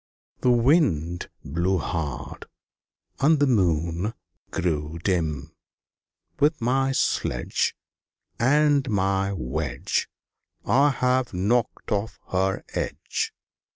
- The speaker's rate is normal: No, slow, 90 wpm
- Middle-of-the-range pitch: No, very low, 95 Hz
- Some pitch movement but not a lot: No, wide, 7.5 semitones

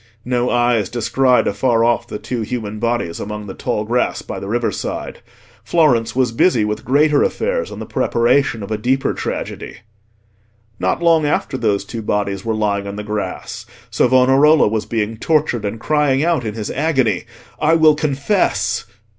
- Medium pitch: No, low, 120 Hz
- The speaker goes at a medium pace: Yes, average, 165 wpm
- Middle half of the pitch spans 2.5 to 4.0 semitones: No, average, 4.7 semitones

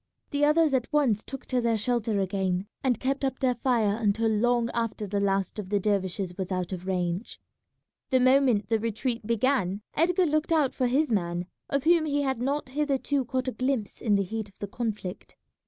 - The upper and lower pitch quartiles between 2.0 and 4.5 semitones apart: No, average, 5.1 semitones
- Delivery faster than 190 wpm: Yes, average, 200 wpm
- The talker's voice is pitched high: Yes, high, 230 Hz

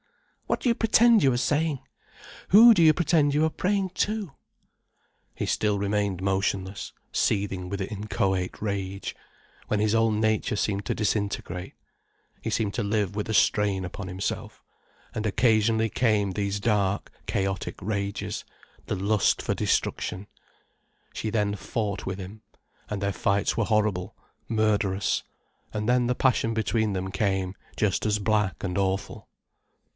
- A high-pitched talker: No, low, 105 Hz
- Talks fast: No, average, 145 wpm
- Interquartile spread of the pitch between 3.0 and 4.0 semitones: No, narrow, 2.5 semitones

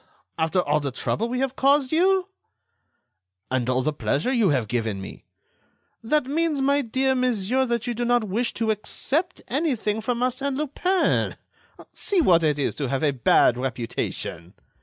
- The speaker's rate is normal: Yes, average, 165 wpm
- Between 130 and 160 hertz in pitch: No, high, 235 Hz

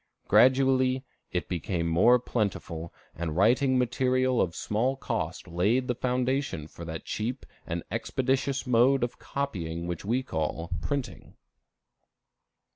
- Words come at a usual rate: No, slow, 120 wpm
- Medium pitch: No, low, 120 Hz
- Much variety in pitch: Yes, wide, 7.2 semitones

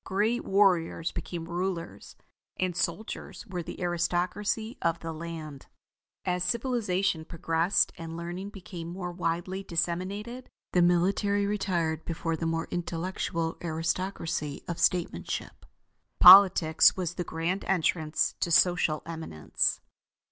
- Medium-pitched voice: Yes, medium, 175 Hz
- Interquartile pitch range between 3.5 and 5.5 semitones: No, narrow, 2.5 semitones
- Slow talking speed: Yes, slow, 115 wpm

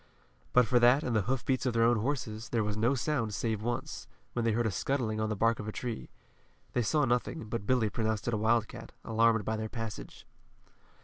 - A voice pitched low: Yes, low, 115 Hz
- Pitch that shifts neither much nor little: No, narrow, 2.0 semitones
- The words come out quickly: Yes, fast, 220 wpm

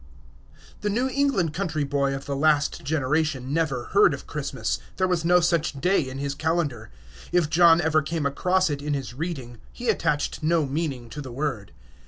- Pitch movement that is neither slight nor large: Yes, average, 3.7 semitones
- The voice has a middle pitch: Yes, medium, 155 Hz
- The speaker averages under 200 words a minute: Yes, average, 185 wpm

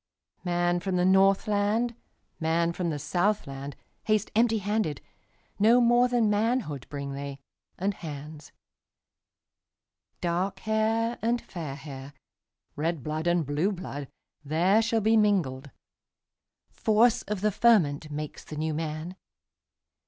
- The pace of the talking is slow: Yes, slow, 95 wpm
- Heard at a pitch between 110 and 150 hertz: No, medium, 180 Hz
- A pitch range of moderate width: No, wide, 6.1 semitones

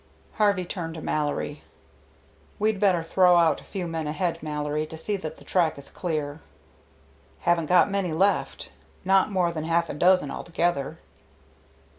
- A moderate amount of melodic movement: Yes, average, 3.0 semitones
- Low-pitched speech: No, medium, 170 Hz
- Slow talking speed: No, average, 155 wpm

